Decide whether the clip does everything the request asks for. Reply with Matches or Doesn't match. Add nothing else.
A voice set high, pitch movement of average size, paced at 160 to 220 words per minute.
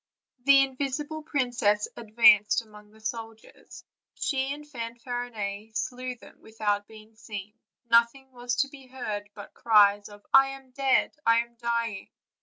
Doesn't match